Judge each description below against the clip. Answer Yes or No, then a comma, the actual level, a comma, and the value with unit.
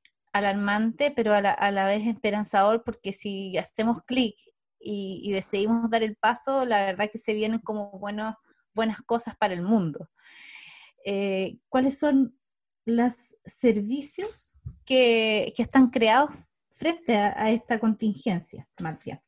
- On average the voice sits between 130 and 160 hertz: No, high, 220 Hz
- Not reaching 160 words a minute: Yes, average, 140 wpm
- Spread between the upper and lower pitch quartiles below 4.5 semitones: Yes, average, 2.9 semitones